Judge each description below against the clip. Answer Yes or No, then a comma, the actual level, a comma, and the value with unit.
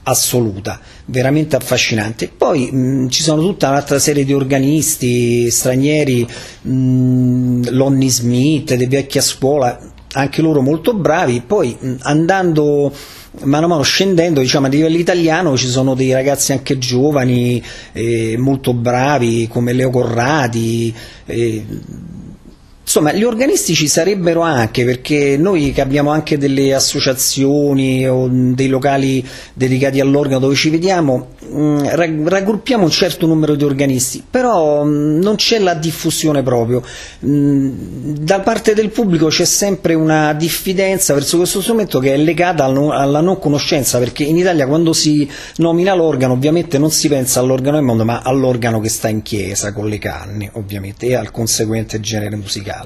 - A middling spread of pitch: Yes, average, 3.9 semitones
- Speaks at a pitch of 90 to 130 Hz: No, medium, 140 Hz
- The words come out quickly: No, average, 145 wpm